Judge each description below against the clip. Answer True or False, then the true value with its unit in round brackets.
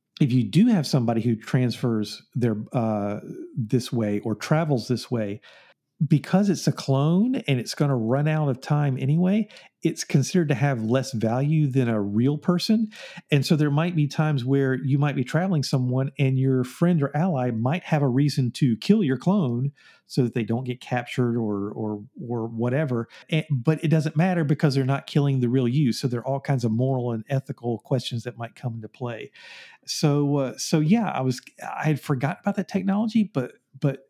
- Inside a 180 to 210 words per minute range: True (200 wpm)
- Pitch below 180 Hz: True (135 Hz)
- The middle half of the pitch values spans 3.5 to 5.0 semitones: True (4.1 semitones)